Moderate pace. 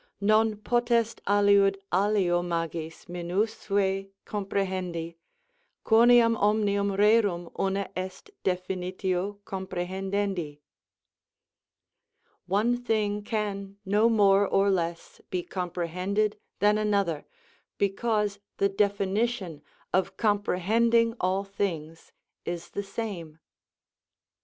No: slow, 85 wpm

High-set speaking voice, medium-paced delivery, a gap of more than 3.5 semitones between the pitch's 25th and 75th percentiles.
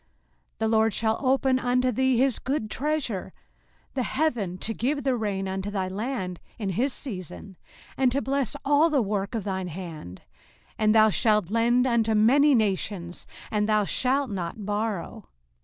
Yes: high, 220 Hz; average, 165 wpm; average, 4.8 semitones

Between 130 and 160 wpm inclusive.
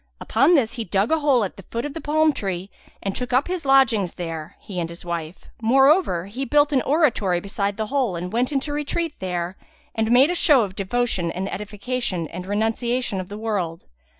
No: fast, 205 wpm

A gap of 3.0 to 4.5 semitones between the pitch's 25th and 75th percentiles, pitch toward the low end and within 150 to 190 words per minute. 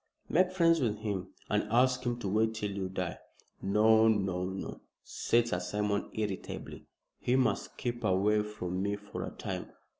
Yes: average, 3.3 semitones; low, 105 Hz; average, 170 wpm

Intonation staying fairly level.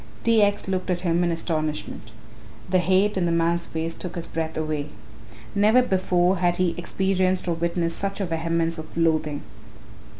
Yes: narrow, 2.2 semitones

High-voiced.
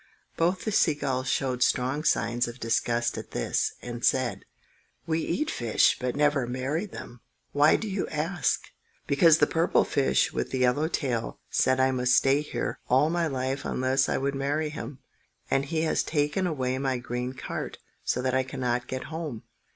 No: low, 135 Hz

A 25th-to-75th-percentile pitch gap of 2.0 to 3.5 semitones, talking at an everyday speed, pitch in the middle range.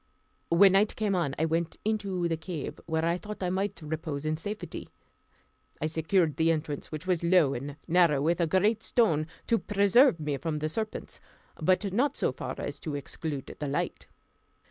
No: average, 4.1 semitones; average, 185 wpm; medium, 170 Hz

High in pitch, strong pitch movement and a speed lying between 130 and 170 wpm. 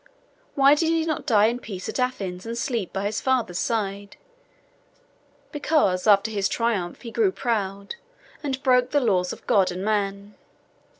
No: high, 220 Hz; average, 4.8 semitones; average, 165 wpm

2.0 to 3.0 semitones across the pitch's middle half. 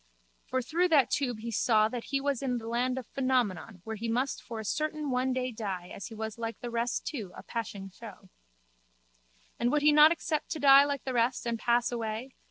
No: average, 3.4 semitones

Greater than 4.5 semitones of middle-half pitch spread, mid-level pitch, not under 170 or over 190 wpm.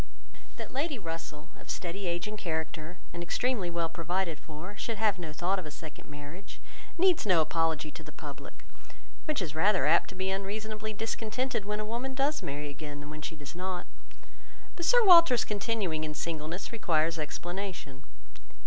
Yes: average, 5.1 semitones; medium, 180 Hz; average, 175 wpm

